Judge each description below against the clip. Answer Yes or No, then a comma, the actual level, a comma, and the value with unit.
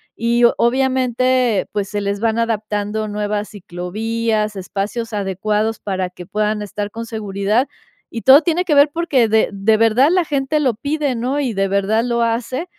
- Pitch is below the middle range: No, high, 225 Hz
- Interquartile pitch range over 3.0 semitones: Yes, average, 3.6 semitones